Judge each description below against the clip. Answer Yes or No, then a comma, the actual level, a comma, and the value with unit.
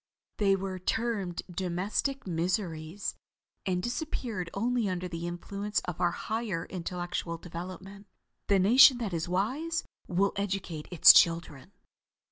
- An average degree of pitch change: Yes, average, 3.2 semitones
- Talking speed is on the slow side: Yes, slow, 120 wpm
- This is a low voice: No, medium, 185 Hz